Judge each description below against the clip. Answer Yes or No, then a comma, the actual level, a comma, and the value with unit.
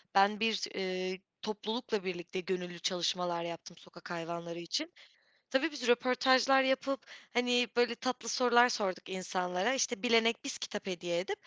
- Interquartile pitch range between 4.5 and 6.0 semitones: Yes, wide, 5.4 semitones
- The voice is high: Yes, high, 210 Hz